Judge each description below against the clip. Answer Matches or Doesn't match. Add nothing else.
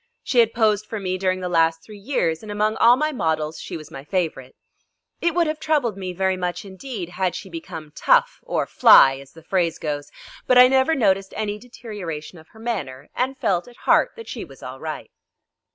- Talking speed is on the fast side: Matches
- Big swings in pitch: Matches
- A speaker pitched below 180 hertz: Doesn't match